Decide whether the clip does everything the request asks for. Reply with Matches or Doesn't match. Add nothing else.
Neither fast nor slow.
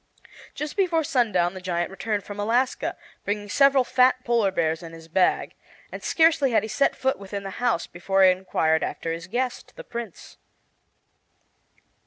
Matches